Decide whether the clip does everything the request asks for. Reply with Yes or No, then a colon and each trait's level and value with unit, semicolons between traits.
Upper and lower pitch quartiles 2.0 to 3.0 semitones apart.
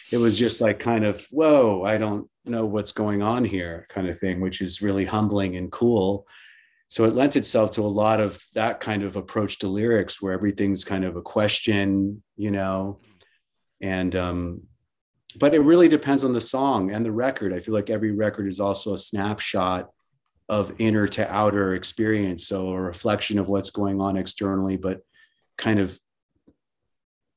Yes: narrow, 2.5 semitones